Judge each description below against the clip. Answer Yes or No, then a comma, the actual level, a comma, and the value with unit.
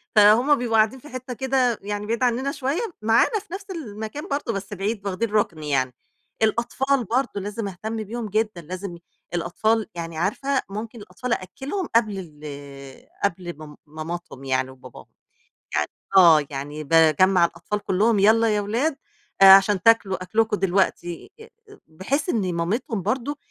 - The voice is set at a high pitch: Yes, high, 210 Hz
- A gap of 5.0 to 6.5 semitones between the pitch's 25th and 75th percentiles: Yes, average, 5.3 semitones